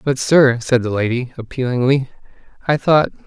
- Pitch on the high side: No, low, 130 Hz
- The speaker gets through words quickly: No, average, 145 wpm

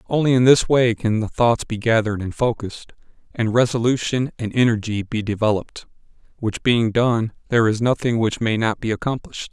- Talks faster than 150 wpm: Yes, average, 175 wpm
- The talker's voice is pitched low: Yes, low, 115 Hz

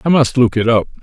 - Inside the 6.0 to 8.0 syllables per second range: Yes, 6.3 syllables/s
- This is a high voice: No, low, 125 Hz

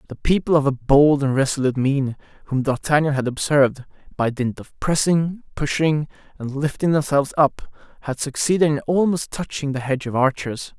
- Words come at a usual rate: Yes, average, 165 wpm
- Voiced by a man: Yes, male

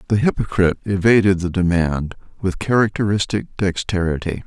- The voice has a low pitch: Yes, very low, 95 Hz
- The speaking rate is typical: No, slow, 110 wpm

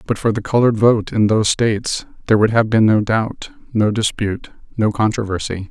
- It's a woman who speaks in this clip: No, male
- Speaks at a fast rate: No, average, 190 wpm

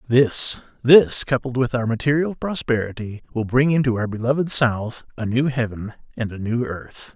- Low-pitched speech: Yes, low, 125 Hz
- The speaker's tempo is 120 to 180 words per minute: Yes, average, 170 wpm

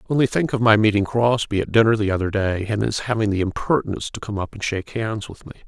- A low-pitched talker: Yes, low, 110 Hz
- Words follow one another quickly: Yes, fast, 255 wpm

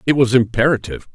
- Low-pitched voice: Yes, low, 120 Hz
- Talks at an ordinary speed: Yes, average, 155 wpm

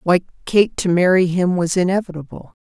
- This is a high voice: No, medium, 180 Hz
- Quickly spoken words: No, average, 160 wpm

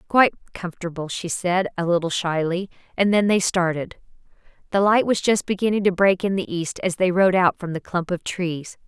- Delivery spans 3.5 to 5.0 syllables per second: No, 5.3 syllables/s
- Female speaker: Yes, female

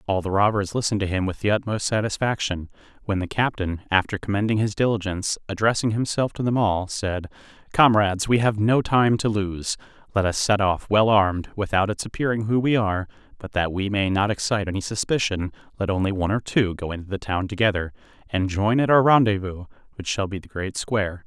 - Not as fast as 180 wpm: No, average, 200 wpm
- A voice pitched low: Yes, low, 100 Hz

